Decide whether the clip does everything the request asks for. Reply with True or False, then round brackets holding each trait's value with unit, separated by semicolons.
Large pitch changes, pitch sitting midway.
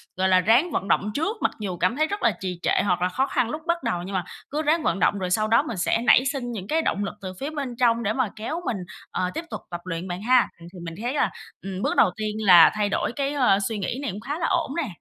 False (6.7 semitones; 225 Hz)